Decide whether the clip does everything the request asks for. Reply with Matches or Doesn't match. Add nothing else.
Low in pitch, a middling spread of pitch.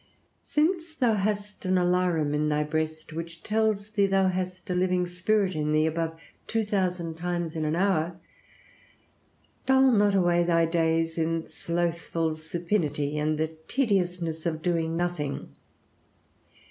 Doesn't match